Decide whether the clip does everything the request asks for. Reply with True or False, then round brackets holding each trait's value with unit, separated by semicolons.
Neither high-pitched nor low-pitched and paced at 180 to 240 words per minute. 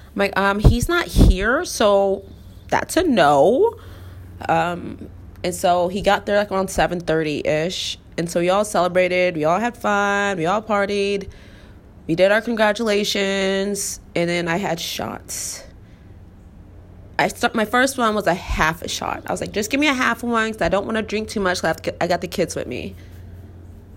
True (180 Hz; 200 wpm)